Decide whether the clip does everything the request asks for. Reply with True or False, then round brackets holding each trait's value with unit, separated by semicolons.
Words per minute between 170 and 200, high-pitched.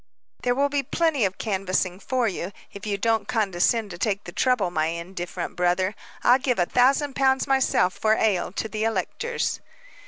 True (175 wpm; 215 Hz)